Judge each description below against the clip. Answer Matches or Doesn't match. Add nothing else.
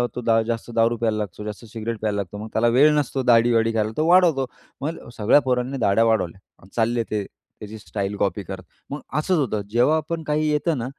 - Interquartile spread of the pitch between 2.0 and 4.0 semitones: Doesn't match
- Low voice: Matches